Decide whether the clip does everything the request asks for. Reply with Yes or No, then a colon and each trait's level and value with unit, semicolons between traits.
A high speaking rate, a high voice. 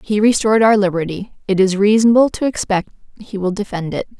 No: average, 185 wpm; high, 205 Hz